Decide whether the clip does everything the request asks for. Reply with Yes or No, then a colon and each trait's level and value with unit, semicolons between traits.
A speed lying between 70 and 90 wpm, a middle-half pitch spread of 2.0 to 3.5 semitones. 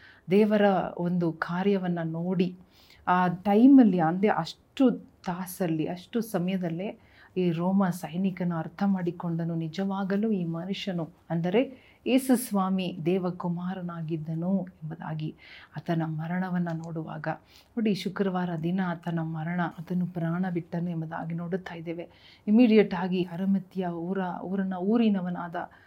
No: average, 100 wpm; narrow, 2.4 semitones